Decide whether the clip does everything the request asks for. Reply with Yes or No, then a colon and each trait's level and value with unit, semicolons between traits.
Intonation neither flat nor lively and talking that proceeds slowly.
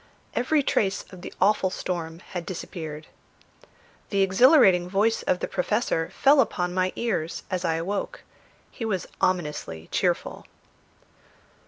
Yes: average, 3.8 semitones; slow, 130 wpm